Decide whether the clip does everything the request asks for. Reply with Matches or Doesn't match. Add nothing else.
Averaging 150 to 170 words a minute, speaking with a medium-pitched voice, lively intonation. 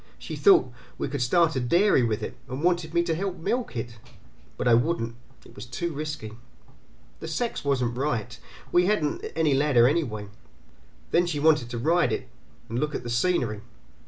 Doesn't match